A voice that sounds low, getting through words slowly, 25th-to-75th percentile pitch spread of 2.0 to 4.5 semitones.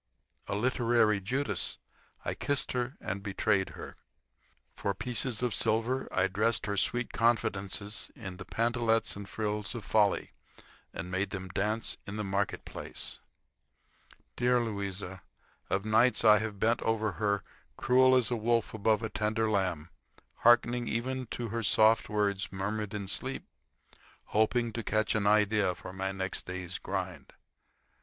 No: low, 110 Hz; average, 150 wpm; average, 2.8 semitones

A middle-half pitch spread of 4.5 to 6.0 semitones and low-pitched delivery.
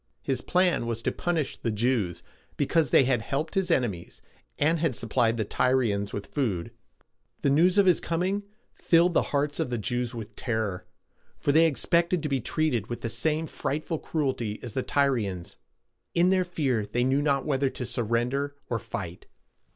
Yes: average, 5.3 semitones; low, 130 Hz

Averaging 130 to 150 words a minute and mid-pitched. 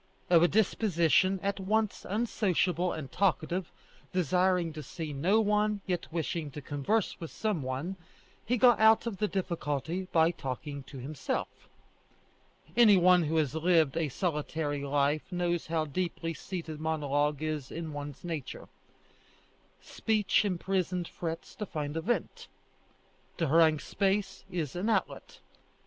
Yes: average, 140 wpm; medium, 170 Hz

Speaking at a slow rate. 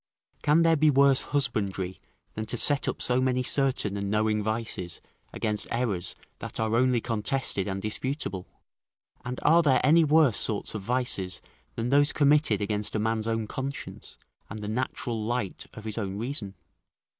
No: average, 165 wpm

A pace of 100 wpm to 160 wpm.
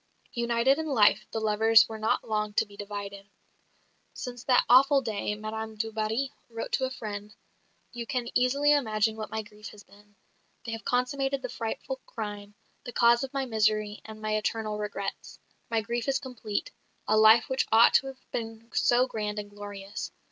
No: average, 180 wpm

